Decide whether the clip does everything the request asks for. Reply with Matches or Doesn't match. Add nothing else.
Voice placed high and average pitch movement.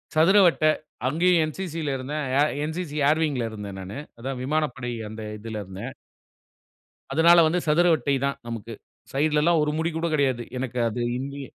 Doesn't match